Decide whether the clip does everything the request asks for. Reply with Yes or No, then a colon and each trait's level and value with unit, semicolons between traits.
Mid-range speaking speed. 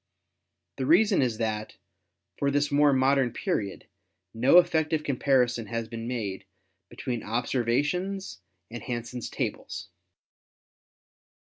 No: slow, 110 wpm